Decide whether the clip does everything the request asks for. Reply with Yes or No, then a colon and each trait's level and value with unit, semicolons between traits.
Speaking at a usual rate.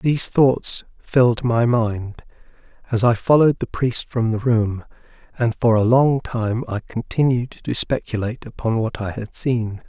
Yes: average, 165 wpm